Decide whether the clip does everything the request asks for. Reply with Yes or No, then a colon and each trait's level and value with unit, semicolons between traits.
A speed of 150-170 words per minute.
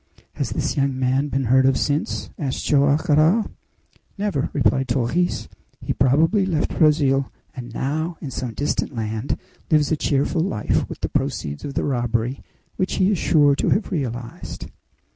Yes: average, 160 wpm